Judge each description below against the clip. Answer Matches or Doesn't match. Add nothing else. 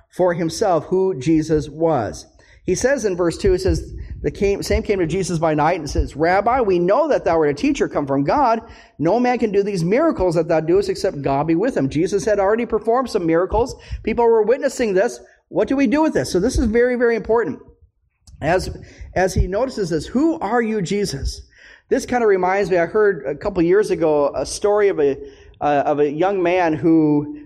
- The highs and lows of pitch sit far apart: Matches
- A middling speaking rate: Doesn't match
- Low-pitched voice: Doesn't match